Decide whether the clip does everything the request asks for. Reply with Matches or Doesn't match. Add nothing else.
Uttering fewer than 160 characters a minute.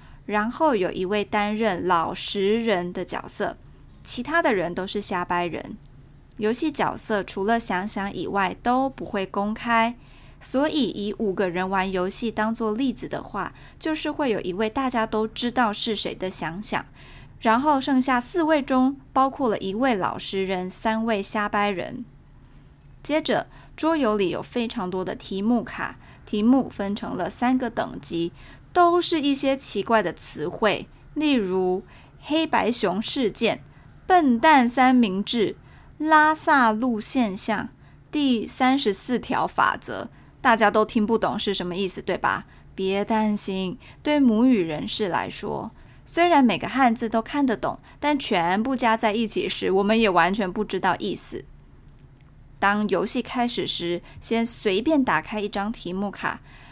Doesn't match